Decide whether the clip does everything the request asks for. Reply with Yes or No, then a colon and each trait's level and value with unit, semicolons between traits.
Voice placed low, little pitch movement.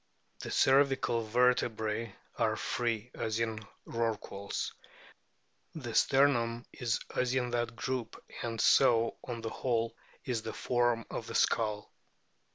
Yes: low, 115 Hz; narrow, 1.6 semitones